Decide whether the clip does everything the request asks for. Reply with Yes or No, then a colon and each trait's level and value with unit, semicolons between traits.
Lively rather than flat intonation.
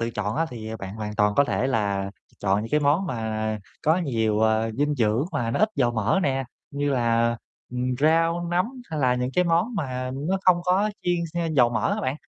Yes: wide, 6.2 semitones